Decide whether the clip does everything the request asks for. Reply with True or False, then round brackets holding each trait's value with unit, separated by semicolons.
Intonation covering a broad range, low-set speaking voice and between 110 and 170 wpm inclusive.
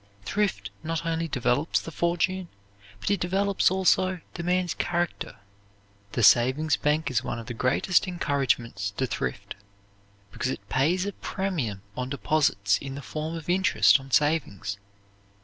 False (6.0 semitones; 155 Hz; 150 wpm)